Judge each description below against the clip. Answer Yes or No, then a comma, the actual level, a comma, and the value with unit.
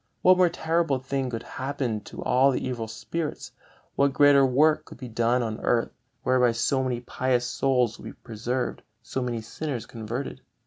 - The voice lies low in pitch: Yes, low, 130 Hz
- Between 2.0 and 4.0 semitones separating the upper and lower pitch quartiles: Yes, average, 2.7 semitones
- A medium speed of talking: Yes, average, 175 wpm